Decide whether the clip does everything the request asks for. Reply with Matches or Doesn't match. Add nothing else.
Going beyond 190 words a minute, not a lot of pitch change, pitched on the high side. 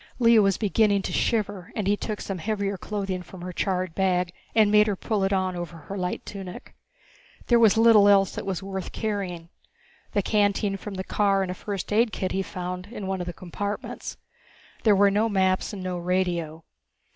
Matches